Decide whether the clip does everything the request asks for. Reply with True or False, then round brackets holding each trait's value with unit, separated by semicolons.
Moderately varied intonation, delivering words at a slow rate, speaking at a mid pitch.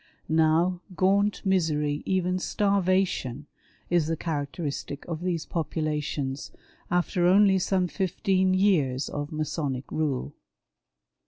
True (4.0 semitones; 100 wpm; 170 Hz)